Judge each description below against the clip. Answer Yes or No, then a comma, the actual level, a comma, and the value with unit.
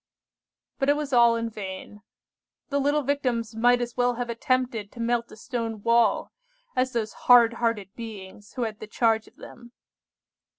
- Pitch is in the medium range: No, high, 235 Hz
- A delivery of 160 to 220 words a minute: Yes, average, 170 wpm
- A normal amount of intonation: No, narrow, 1.9 semitones